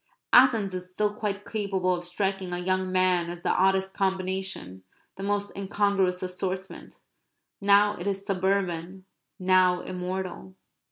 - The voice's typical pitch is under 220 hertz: Yes, high, 190 Hz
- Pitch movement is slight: Yes, narrow, 1.5 semitones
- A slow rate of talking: Yes, slow, 130 wpm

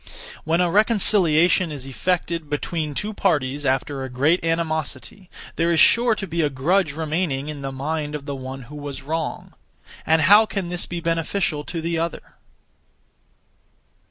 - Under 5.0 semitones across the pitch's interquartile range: Yes, average, 3.4 semitones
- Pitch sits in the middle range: Yes, medium, 160 Hz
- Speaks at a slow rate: No, average, 160 wpm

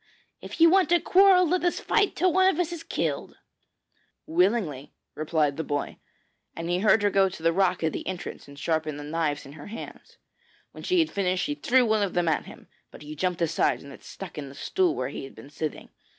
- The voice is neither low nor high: Yes, medium, 180 Hz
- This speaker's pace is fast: Yes, fast, 230 wpm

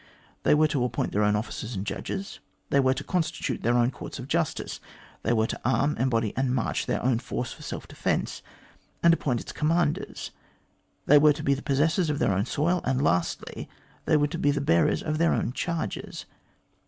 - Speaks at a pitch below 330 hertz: Yes, medium, 140 Hz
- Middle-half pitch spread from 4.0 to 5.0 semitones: Yes, average, 4.5 semitones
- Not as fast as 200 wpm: No, fast, 205 wpm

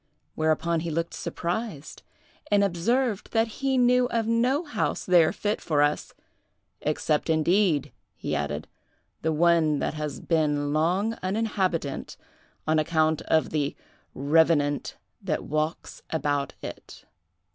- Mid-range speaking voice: Yes, medium, 165 Hz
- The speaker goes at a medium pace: No, slow, 125 wpm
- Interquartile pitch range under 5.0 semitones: No, wide, 5.4 semitones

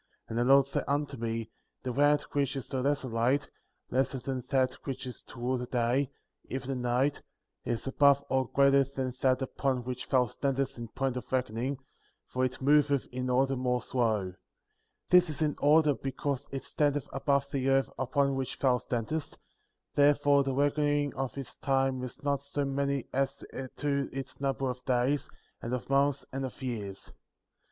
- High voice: No, low, 135 Hz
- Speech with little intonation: Yes, narrow, 1.8 semitones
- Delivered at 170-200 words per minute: Yes, average, 180 wpm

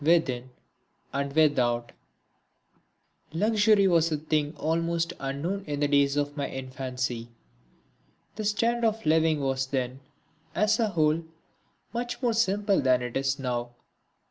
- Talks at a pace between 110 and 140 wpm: Yes, slow, 135 wpm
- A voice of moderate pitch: Yes, medium, 150 Hz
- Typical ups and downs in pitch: No, wide, 6.7 semitones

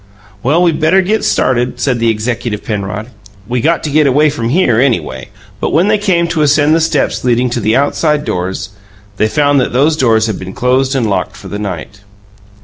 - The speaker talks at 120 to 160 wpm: No, fast, 205 wpm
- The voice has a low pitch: Yes, low, 125 Hz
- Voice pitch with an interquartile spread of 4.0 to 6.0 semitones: Yes, wide, 5.5 semitones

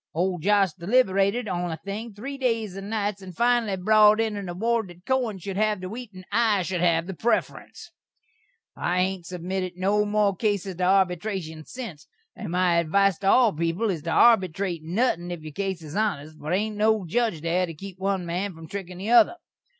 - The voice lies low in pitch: No, high, 195 Hz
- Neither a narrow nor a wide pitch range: Yes, average, 3.4 semitones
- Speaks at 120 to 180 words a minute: No, average, 200 wpm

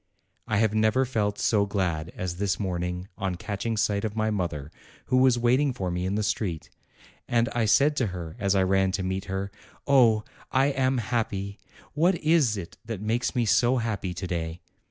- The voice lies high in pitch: No, low, 105 Hz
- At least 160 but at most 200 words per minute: Yes, average, 195 wpm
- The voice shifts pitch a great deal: No, average, 4.1 semitones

